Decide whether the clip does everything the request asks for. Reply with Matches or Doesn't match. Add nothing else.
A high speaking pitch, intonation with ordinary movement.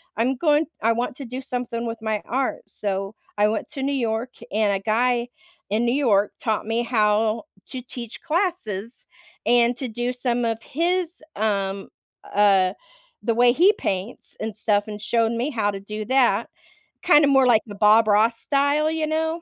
Matches